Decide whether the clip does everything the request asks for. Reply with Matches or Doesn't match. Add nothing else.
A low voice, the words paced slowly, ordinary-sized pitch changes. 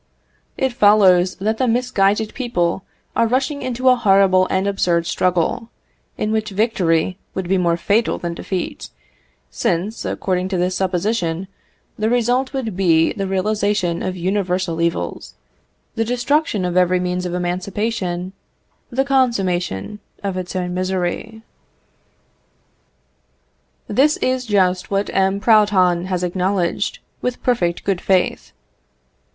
Doesn't match